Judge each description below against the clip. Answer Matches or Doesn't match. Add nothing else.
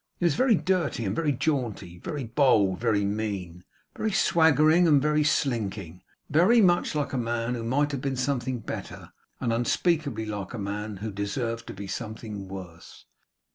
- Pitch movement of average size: Doesn't match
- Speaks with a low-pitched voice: Matches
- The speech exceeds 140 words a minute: Matches